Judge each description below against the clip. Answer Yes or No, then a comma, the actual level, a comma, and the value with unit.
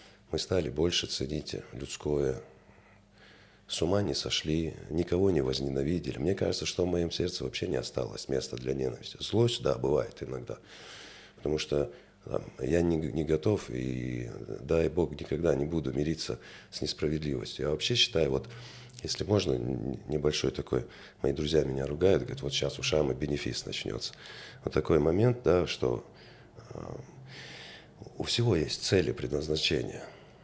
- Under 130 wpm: No, average, 145 wpm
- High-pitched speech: No, very low, 80 Hz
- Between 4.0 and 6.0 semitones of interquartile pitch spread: Yes, average, 4.9 semitones